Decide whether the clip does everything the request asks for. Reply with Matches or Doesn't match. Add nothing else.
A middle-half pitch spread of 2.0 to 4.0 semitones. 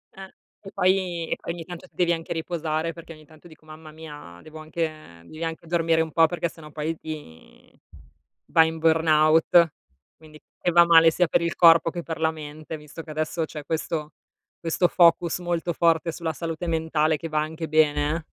Doesn't match